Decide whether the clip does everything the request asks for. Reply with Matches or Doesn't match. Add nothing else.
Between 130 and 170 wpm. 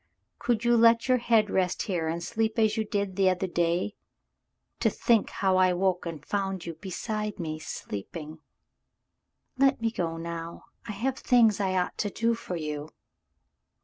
Doesn't match